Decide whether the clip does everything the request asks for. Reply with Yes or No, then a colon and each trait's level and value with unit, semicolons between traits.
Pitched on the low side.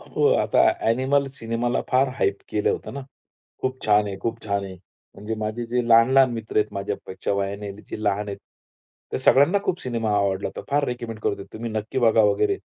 Yes: low, 110 Hz